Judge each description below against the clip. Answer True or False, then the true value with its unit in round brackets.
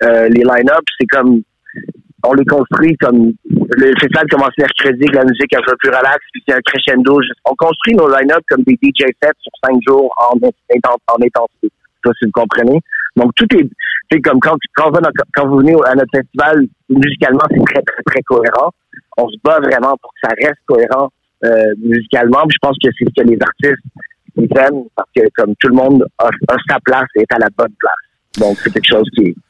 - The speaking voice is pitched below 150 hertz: True (135 Hz)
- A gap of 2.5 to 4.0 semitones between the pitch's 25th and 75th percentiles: True (3.2 semitones)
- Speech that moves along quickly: True (225 wpm)